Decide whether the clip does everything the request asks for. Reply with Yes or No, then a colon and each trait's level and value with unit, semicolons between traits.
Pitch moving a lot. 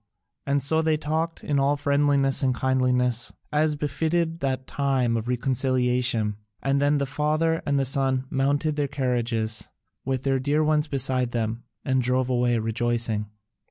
No: average, 2.7 semitones